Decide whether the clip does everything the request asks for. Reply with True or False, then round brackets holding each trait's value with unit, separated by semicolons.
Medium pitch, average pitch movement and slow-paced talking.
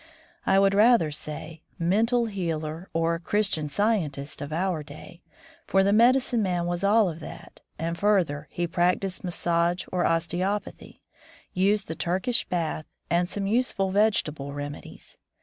False (175 Hz; 3.8 semitones; 145 wpm)